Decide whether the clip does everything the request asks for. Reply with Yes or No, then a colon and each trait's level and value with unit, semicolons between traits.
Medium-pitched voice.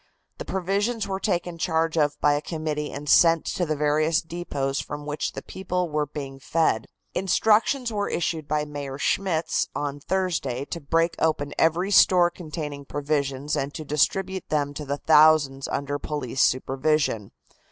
Yes: medium, 155 Hz